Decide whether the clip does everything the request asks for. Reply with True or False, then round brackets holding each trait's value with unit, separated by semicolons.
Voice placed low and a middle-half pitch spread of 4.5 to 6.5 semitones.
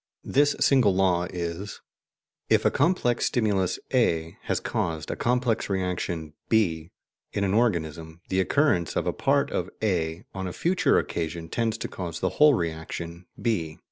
True (90 Hz; 5.1 semitones)